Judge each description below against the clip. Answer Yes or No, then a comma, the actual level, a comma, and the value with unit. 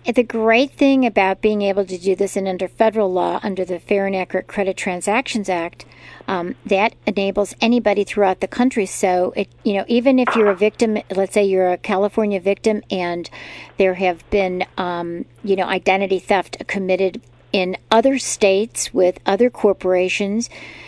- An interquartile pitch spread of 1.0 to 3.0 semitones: Yes, narrow, 2.5 semitones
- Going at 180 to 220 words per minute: No, average, 170 wpm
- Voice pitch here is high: Yes, high, 195 Hz